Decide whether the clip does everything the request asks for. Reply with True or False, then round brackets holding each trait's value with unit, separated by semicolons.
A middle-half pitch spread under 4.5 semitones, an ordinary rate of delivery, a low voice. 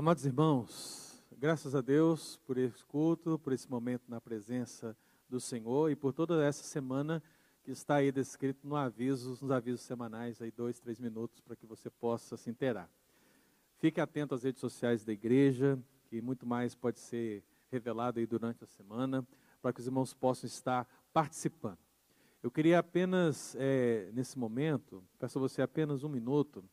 True (3.1 semitones; 170 wpm; 130 Hz)